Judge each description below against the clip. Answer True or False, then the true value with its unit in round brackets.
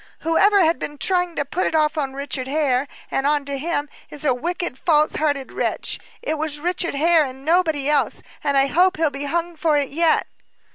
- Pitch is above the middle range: True (300 Hz)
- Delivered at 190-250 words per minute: True (200 wpm)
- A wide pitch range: False (3.1 semitones)